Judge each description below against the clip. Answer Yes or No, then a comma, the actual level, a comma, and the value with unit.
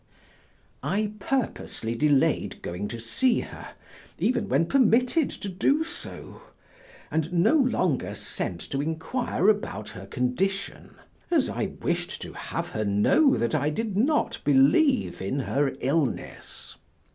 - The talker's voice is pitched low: No, medium, 170 Hz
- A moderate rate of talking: No, slow, 130 wpm